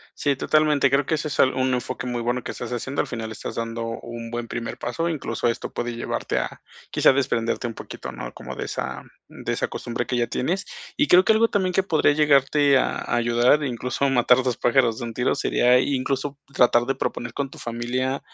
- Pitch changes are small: No, average, 3.0 semitones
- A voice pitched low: Yes, low, 125 Hz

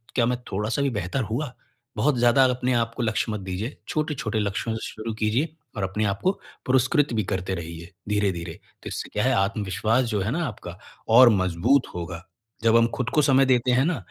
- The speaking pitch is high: No, low, 115 Hz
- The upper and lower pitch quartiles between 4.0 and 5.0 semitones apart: Yes, average, 4.6 semitones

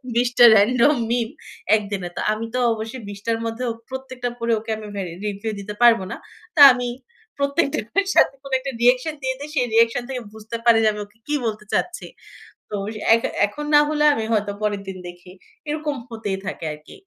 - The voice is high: Yes, high, 230 Hz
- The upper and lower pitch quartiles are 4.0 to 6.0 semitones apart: No, average, 3.6 semitones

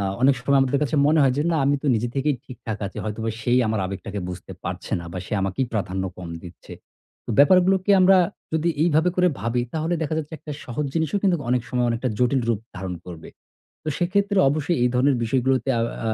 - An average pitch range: No, wide, 6.0 semitones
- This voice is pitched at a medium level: No, low, 130 Hz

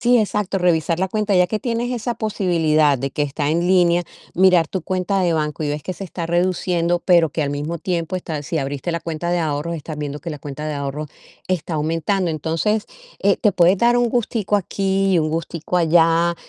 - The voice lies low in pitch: No, medium, 170 Hz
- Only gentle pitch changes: No, average, 3.5 semitones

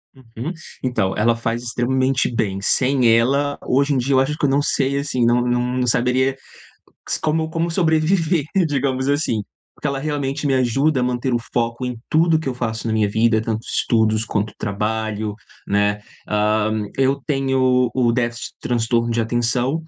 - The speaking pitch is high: No, low, 125 Hz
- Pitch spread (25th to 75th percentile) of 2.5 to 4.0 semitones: Yes, average, 3.3 semitones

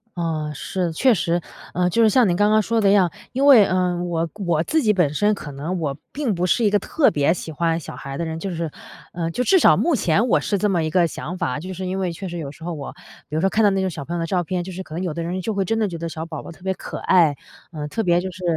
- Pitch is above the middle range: No, medium, 180 Hz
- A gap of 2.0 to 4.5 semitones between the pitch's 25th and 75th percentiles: Yes, average, 3.5 semitones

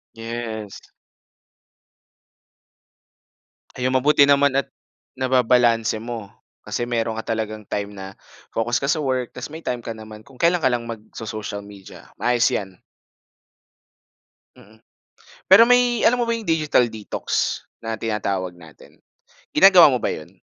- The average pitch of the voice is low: Yes, low, 115 Hz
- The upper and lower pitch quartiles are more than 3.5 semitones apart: Yes, average, 4.2 semitones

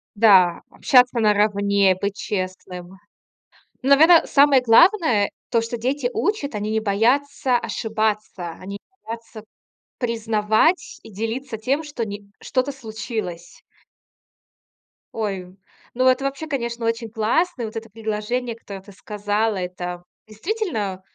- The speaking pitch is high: Yes, high, 225 Hz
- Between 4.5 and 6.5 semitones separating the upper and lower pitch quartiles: No, average, 3.9 semitones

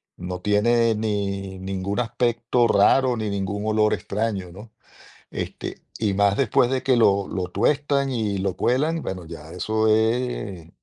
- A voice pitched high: No, low, 105 Hz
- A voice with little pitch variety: No, average, 3.4 semitones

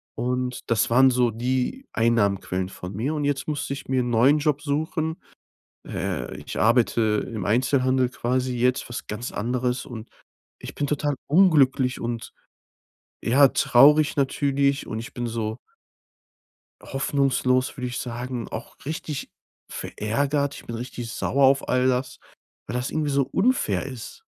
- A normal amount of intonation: Yes, average, 3.0 semitones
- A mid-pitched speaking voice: No, low, 125 Hz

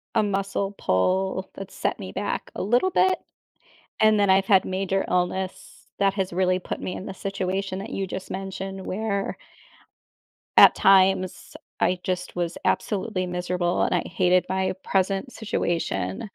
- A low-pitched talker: No, high, 190 Hz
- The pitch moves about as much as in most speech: No, narrow, 1.2 semitones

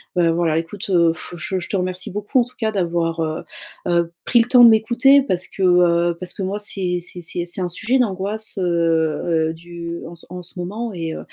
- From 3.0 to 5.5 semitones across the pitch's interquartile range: Yes, average, 3.3 semitones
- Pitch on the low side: No, medium, 180 Hz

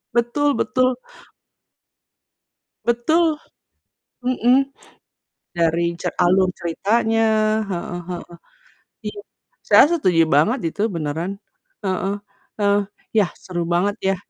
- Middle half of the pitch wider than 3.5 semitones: Yes, wide, 5.4 semitones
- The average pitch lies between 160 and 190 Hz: No, high, 200 Hz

